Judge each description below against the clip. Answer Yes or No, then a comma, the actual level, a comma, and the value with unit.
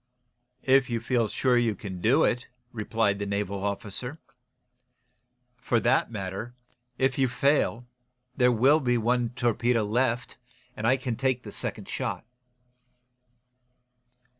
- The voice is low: Yes, low, 120 Hz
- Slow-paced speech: Yes, slow, 130 wpm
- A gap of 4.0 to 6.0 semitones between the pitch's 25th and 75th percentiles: No, average, 2.8 semitones